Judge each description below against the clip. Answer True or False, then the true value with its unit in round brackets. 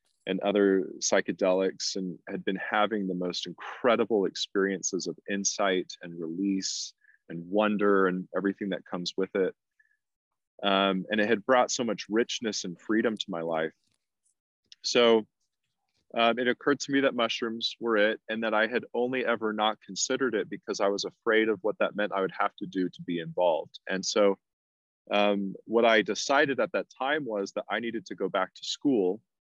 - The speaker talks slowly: False (180 wpm)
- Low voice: True (100 Hz)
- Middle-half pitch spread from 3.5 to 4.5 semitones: False (3.0 semitones)